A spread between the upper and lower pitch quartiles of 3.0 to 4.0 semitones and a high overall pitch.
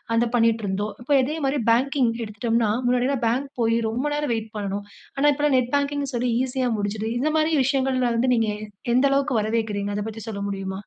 Yes: average, 3.5 semitones; high, 240 Hz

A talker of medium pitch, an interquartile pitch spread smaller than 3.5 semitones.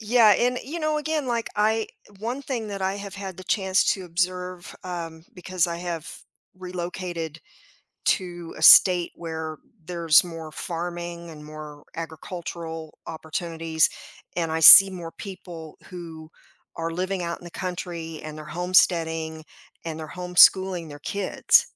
Yes: medium, 175 Hz; average, 2.7 semitones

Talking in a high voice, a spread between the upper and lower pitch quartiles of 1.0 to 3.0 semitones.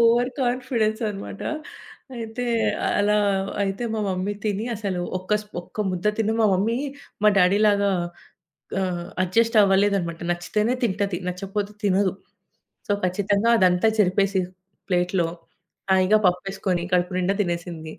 Yes: high, 195 Hz; average, 2.7 semitones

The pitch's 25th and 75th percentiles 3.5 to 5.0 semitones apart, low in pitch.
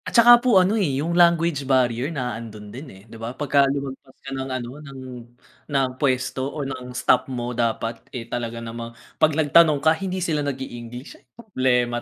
Yes: average, 4.1 semitones; low, 130 Hz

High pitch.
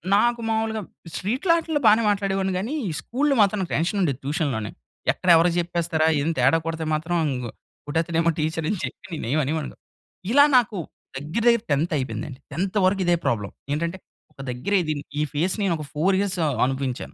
No: medium, 170 Hz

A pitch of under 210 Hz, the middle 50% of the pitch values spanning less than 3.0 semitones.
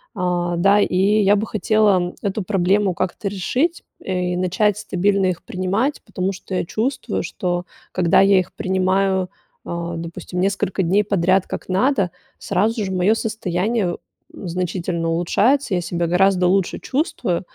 Yes: high, 190 Hz; narrow, 2.5 semitones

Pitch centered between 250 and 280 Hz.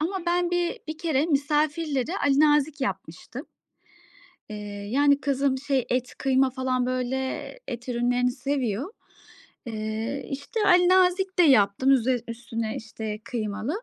Yes: very high, 270 Hz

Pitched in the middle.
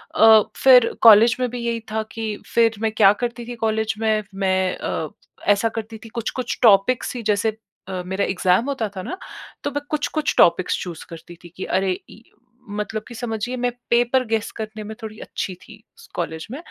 No: high, 220 Hz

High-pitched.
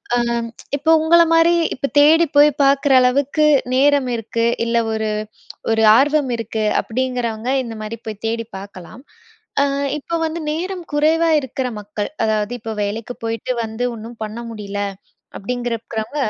Yes: high, 240 Hz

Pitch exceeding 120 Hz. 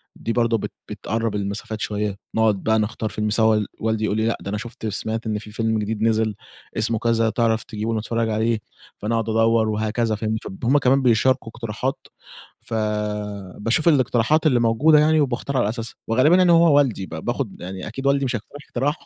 No: low, 115 Hz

